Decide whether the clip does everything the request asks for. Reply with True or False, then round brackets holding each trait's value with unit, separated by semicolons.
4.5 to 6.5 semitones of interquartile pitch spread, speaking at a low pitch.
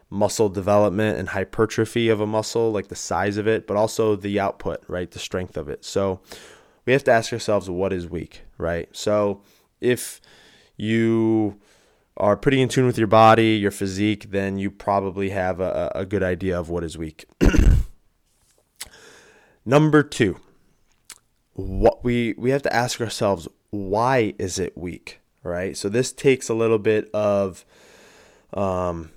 False (2.7 semitones; 105 Hz)